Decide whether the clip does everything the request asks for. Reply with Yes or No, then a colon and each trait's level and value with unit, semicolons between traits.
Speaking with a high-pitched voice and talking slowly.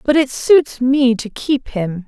No: very high, 255 Hz; average, 200 wpm